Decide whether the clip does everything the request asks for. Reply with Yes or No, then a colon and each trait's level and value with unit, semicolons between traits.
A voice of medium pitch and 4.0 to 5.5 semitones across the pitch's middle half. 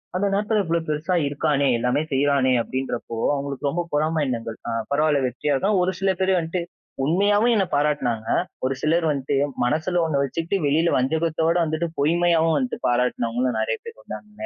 Yes: medium, 150 Hz; average, 4.5 semitones